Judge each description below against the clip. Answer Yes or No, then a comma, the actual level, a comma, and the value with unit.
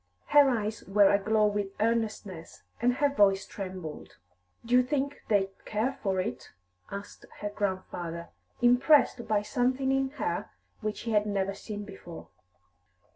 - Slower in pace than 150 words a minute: Yes, average, 140 wpm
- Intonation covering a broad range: No, average, 4.0 semitones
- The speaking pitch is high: Yes, high, 210 Hz